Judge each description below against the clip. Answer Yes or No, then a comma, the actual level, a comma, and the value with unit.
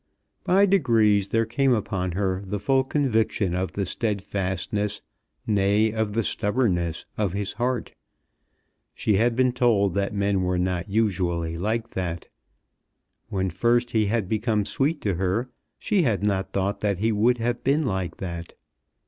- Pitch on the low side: Yes, low, 105 Hz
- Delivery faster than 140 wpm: Yes, average, 155 wpm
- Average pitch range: Yes, average, 3.7 semitones